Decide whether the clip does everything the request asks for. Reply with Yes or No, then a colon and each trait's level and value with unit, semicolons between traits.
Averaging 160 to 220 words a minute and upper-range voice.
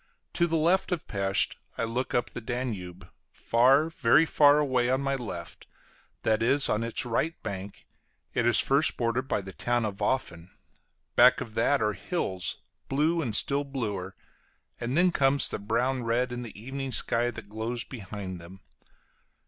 No: average, 170 wpm; low, 120 Hz